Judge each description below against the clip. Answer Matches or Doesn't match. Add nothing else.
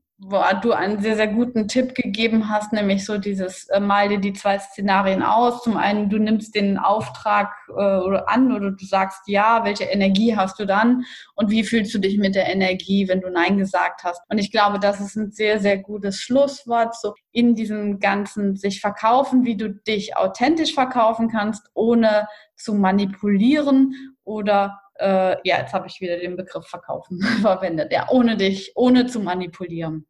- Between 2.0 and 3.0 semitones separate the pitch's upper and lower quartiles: Matches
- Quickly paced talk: Doesn't match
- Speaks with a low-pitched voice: Doesn't match